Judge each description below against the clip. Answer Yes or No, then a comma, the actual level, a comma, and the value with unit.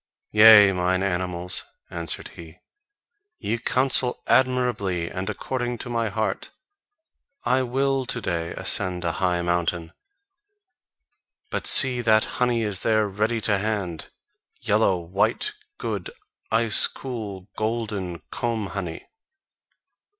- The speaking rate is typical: No, slow, 115 wpm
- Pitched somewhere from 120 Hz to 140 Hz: No, low, 105 Hz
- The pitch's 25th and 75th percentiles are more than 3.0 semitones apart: Yes, average, 4.7 semitones